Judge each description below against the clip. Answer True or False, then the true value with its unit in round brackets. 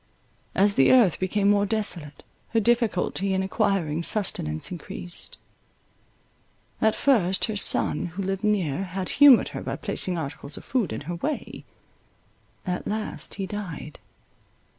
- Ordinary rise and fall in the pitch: True (3.4 semitones)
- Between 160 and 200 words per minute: False (140 wpm)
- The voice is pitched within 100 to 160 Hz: False (195 Hz)